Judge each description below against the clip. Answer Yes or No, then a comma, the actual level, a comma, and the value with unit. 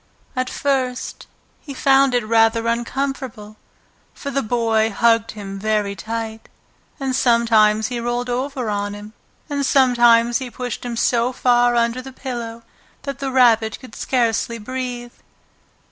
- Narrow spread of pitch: Yes, narrow, 2.3 semitones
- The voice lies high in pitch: Yes, high, 240 Hz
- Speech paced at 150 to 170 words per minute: No, average, 140 wpm